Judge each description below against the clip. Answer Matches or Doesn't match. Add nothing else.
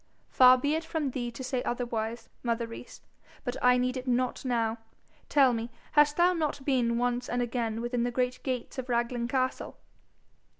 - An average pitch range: Doesn't match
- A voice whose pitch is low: Doesn't match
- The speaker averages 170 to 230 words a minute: Matches